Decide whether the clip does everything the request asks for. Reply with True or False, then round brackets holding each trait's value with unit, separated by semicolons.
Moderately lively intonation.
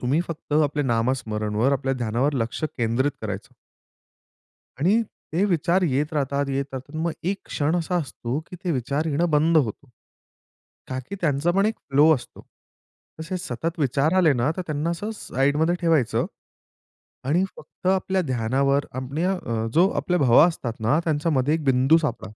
True (4.5 semitones)